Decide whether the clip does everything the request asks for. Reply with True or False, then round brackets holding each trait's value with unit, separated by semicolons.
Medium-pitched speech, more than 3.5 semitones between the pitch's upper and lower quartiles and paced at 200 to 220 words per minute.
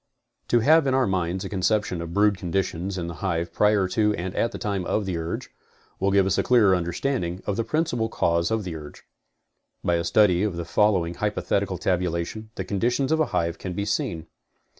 False (95 Hz; 3.9 semitones; 205 wpm)